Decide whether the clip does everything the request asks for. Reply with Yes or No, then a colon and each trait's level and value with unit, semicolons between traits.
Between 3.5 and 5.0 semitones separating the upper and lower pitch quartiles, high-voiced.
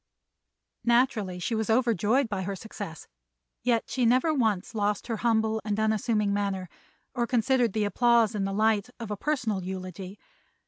No: average, 2.9 semitones; high, 220 Hz